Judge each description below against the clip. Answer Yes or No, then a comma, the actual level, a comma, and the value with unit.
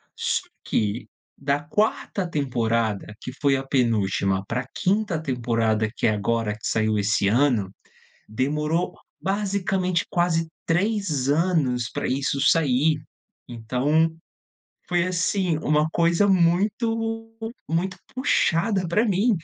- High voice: No, medium, 150 Hz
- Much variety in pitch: Yes, wide, 7.4 semitones